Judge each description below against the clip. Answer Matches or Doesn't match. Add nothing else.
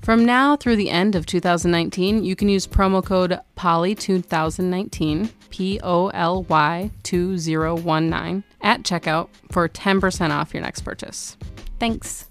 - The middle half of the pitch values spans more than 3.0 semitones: Doesn't match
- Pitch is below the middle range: Doesn't match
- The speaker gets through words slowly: Matches